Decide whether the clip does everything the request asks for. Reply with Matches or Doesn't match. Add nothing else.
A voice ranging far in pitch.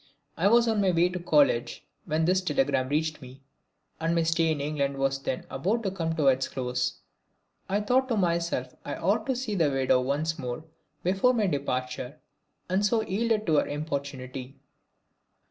Matches